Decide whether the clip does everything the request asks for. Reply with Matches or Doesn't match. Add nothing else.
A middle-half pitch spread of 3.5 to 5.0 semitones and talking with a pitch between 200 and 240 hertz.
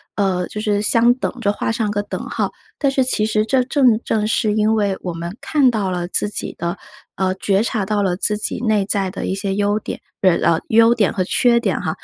Doesn't match